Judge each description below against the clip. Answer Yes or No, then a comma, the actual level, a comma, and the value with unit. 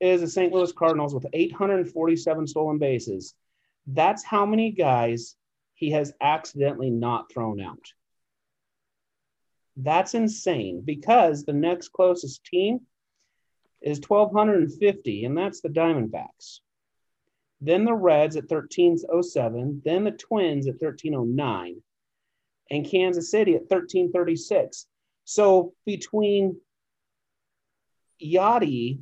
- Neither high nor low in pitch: Yes, medium, 165 Hz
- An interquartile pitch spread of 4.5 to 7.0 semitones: Yes, average, 4.8 semitones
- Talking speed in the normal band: No, slow, 105 wpm